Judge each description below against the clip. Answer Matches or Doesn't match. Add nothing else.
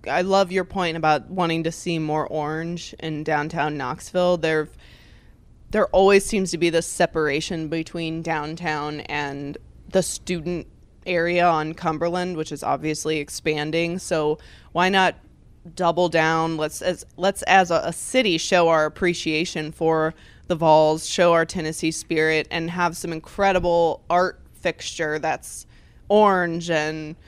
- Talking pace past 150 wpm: Doesn't match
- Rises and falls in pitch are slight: Matches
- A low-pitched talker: Doesn't match